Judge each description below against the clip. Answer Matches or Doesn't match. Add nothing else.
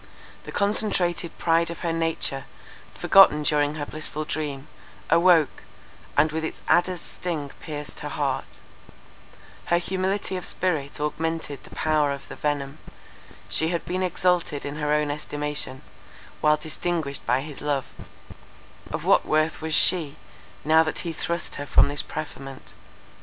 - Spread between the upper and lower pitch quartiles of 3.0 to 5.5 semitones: Doesn't match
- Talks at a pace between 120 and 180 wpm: Matches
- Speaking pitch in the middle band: Matches